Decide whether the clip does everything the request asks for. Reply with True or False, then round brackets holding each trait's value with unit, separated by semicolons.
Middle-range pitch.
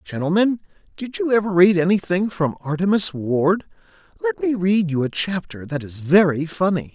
True (175 Hz)